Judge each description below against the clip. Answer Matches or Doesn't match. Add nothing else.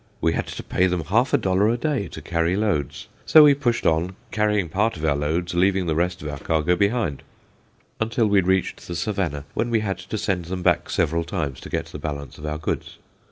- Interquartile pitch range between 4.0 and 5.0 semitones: Matches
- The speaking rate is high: Matches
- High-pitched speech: Doesn't match